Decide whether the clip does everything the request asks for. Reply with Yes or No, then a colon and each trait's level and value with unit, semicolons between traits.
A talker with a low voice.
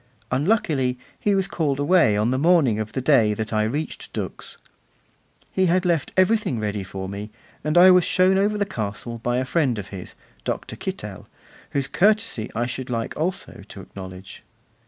Yes: low, 130 Hz